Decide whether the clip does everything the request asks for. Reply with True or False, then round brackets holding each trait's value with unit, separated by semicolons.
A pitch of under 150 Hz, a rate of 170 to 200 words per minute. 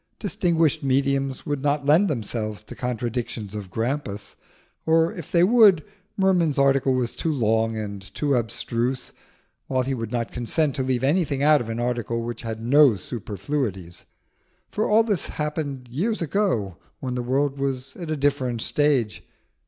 False (135 Hz; 160 wpm)